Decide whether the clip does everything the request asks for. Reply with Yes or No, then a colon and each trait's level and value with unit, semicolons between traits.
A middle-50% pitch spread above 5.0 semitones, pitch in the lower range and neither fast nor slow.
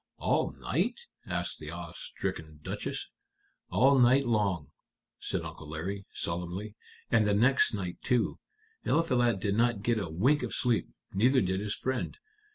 Yes: wide, 5.5 semitones; low, 105 Hz; average, 150 wpm